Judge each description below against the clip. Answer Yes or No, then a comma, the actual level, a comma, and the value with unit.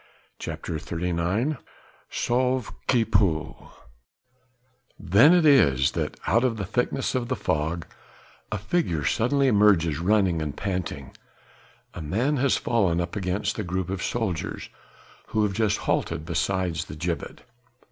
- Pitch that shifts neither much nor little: No, wide, 6.0 semitones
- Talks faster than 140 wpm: No, slow, 135 wpm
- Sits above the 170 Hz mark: No, very low, 95 Hz